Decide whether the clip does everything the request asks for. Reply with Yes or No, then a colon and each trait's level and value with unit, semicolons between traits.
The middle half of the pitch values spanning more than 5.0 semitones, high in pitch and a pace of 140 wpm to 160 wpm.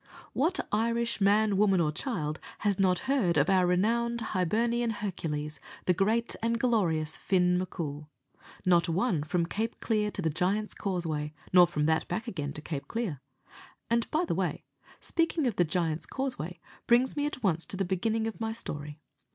No: wide, 5.6 semitones; high, 195 Hz; average, 175 wpm